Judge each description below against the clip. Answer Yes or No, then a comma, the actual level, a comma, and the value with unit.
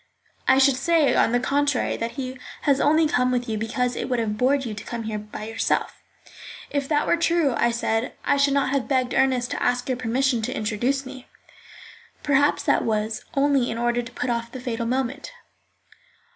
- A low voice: No, very high, 255 Hz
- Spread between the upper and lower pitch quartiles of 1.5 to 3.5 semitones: Yes, average, 2.9 semitones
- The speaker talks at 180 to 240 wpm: Yes, average, 200 wpm